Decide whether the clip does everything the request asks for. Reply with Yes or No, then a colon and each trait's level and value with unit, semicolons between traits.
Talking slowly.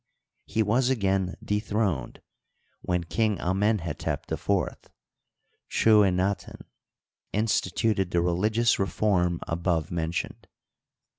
Yes: slow, 85 wpm